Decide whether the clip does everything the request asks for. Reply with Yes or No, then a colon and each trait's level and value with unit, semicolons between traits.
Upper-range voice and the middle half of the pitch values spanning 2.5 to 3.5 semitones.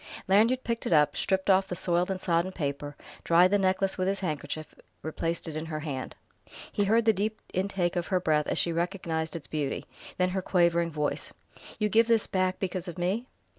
No: medium, 180 Hz; average, 3.1 semitones